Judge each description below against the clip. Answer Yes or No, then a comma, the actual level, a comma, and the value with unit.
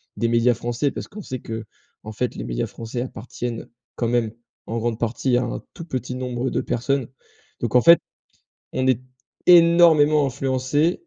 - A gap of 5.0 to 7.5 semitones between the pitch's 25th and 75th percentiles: No, average, 3.2 semitones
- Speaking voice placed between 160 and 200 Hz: No, low, 125 Hz